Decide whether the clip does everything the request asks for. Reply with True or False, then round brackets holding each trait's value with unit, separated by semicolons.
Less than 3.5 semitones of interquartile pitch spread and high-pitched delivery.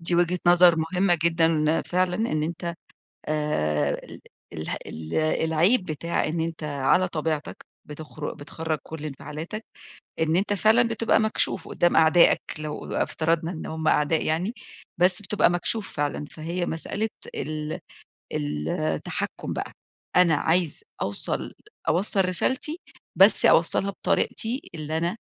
False (2.9 semitones; 165 Hz)